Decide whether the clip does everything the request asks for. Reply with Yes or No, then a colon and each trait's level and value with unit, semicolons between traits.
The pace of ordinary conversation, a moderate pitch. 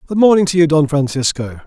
No: fast, 215 wpm; medium, 155 Hz